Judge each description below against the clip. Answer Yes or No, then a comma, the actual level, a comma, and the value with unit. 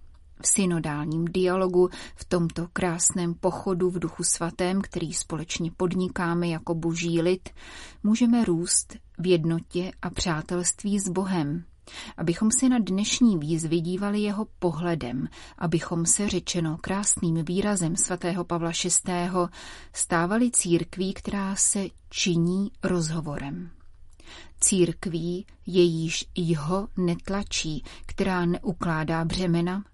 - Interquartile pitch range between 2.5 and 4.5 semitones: No, narrow, 2.1 semitones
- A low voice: No, medium, 175 Hz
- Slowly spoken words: Yes, slow, 105 wpm